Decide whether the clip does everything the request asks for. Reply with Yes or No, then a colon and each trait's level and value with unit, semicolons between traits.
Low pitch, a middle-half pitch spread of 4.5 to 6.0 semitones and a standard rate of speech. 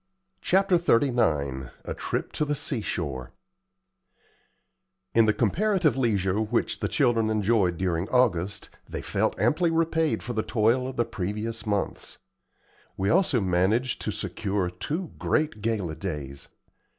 No: low, 110 Hz; wide, 5.6 semitones; slow, 130 wpm